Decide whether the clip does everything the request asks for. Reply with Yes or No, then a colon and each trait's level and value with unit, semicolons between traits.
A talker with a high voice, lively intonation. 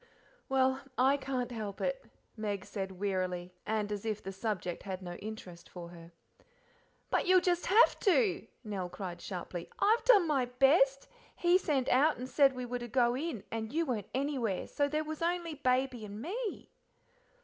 Yes: very high, 250 Hz; wide, 6.9 semitones